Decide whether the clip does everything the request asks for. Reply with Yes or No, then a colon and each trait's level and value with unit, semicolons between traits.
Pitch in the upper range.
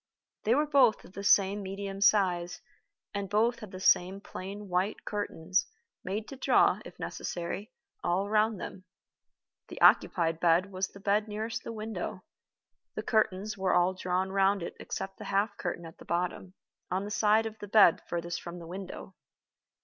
Yes: high, 195 Hz